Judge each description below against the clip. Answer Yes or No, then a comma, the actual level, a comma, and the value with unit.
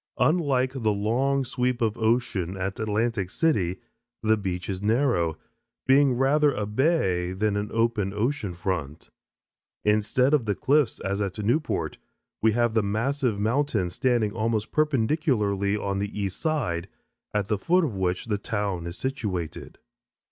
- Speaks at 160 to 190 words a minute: No, average, 150 wpm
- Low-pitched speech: Yes, low, 110 Hz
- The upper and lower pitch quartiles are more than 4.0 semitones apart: Yes, average, 4.7 semitones